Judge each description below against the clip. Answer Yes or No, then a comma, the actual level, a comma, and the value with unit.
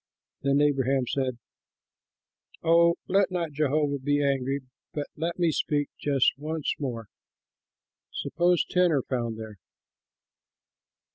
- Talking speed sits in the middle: No, slow, 115 wpm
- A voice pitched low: No, medium, 145 Hz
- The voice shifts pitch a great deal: No, average, 3.4 semitones